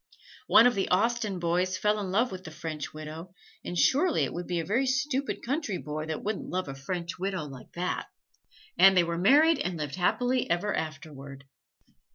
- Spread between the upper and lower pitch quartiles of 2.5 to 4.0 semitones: No, wide, 5.6 semitones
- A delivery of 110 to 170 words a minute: No, average, 195 wpm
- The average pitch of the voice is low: No, medium, 185 Hz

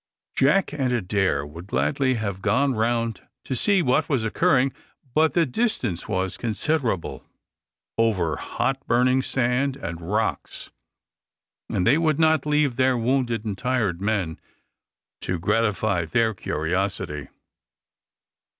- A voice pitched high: No, low, 115 Hz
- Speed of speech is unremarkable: No, slow, 125 wpm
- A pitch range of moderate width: No, wide, 6.0 semitones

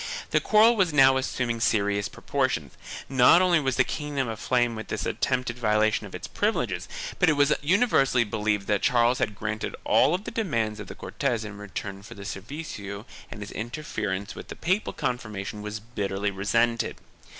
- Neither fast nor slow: Yes, average, 170 wpm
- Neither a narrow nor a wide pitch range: Yes, average, 4.7 semitones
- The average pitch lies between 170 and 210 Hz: No, low, 115 Hz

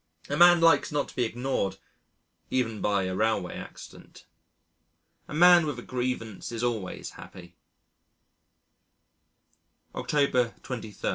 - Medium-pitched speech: No, low, 120 Hz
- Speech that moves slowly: Yes, slow, 120 wpm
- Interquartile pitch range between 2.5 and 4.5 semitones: No, average, 4.9 semitones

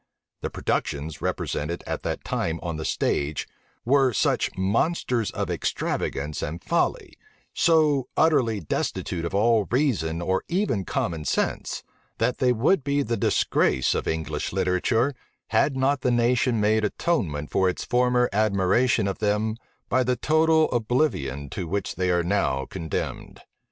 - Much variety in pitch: Yes, wide, 6.8 semitones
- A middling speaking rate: Yes, average, 145 wpm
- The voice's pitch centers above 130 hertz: No, low, 110 Hz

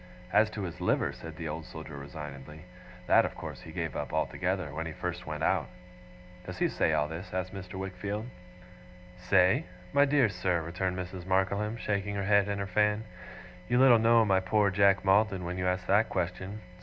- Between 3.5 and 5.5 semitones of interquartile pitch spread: No, narrow, 2.5 semitones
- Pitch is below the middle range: Yes, very low, 95 Hz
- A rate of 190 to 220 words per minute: Yes, average, 195 wpm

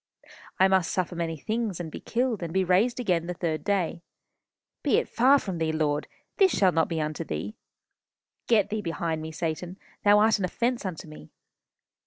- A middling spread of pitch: Yes, average, 4.5 semitones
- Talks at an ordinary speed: Yes, average, 190 wpm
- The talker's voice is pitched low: No, medium, 180 Hz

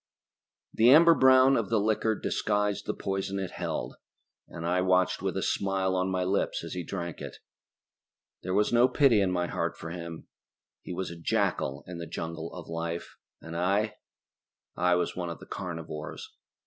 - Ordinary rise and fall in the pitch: Yes, average, 3.3 semitones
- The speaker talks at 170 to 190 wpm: Yes, average, 180 wpm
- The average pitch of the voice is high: No, very low, 95 Hz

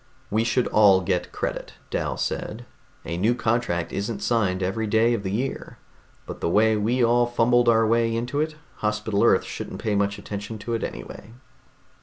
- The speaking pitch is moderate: No, low, 110 Hz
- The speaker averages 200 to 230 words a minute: No, average, 180 wpm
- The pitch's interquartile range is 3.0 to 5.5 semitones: No, narrow, 2.6 semitones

